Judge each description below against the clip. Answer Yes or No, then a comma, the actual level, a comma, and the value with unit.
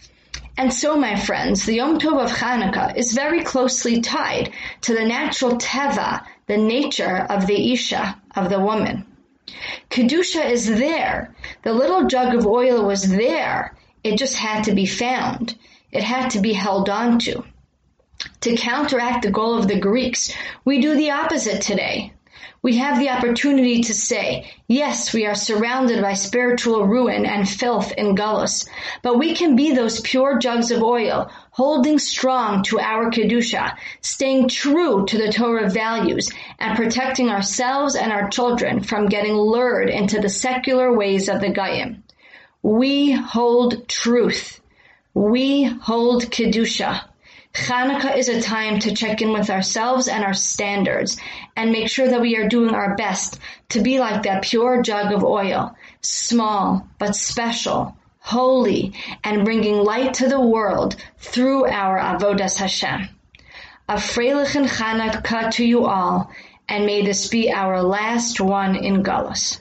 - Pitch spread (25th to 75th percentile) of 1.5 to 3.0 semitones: No, average, 3.5 semitones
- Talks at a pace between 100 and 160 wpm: Yes, average, 150 wpm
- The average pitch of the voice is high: Yes, high, 235 Hz